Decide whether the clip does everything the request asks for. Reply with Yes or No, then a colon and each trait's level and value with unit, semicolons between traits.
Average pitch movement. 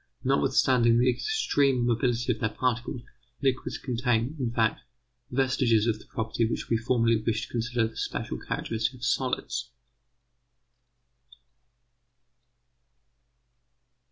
No: narrow, 1.8 semitones